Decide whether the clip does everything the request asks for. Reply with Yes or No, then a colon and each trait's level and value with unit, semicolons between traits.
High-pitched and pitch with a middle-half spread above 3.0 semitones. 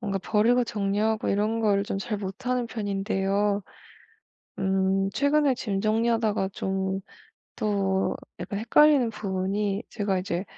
No: high, 205 Hz; narrow, 2.6 semitones